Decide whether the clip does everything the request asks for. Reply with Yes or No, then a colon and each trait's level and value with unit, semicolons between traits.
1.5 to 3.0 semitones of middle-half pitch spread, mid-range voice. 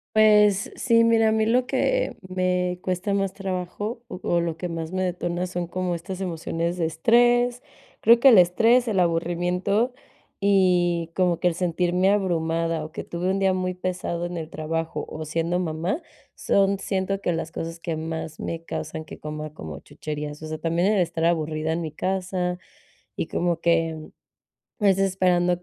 Yes: average, 2.7 semitones; medium, 180 Hz